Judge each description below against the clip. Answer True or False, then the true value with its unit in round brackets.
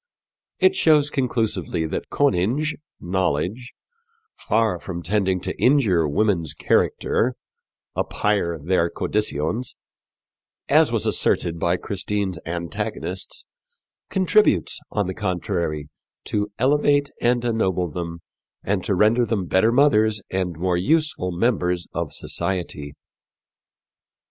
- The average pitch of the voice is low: True (95 Hz)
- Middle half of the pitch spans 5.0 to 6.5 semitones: True (5.3 semitones)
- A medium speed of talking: False (105 wpm)